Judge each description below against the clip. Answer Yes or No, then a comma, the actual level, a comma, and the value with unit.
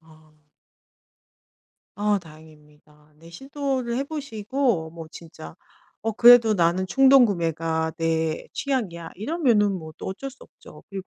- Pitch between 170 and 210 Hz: Yes, high, 190 Hz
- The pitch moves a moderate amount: No, wide, 7.2 semitones